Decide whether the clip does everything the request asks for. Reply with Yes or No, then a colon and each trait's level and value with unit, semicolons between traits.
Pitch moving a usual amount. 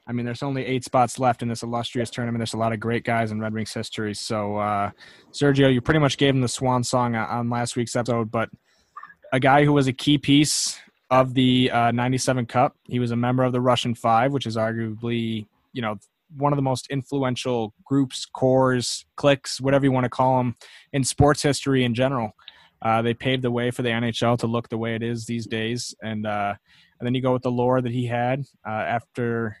No: narrow, 2.2 semitones